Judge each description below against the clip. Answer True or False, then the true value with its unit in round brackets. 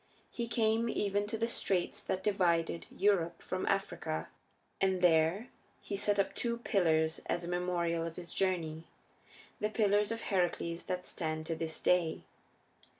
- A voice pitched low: False (180 Hz)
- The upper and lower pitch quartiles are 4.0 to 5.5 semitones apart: False (3.6 semitones)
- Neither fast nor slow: True (150 wpm)